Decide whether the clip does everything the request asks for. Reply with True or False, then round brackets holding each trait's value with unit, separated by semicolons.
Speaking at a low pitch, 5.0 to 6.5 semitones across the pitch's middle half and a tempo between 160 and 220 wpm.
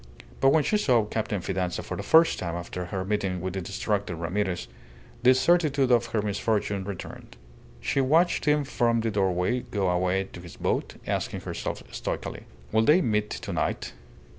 True (105 Hz; 5.4 semitones; 175 wpm)